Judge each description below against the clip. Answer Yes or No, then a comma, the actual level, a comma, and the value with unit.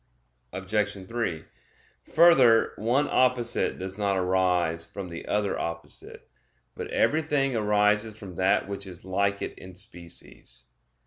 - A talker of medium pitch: No, low, 100 Hz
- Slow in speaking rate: Yes, slow, 125 wpm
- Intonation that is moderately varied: Yes, average, 3.5 semitones